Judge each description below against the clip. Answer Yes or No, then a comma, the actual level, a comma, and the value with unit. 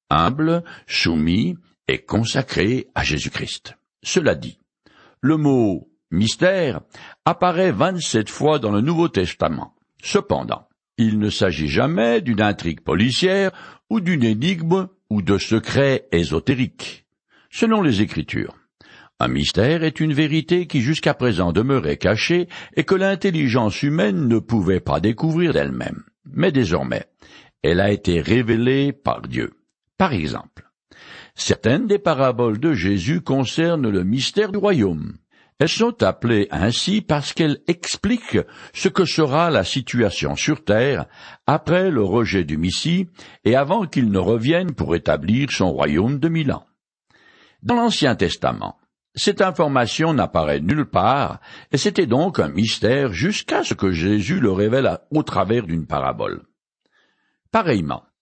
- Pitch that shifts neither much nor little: No, wide, 8.4 semitones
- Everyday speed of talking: No, slow, 135 wpm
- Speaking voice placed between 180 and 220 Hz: No, low, 130 Hz